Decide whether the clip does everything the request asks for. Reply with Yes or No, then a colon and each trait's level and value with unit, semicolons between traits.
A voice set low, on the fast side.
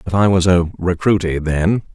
No: very low, 90 Hz; average, 185 wpm